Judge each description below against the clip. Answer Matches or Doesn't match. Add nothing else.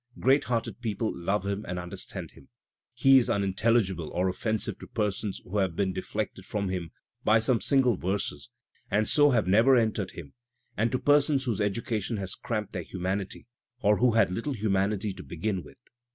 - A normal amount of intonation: Matches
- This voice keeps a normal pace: Matches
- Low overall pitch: Matches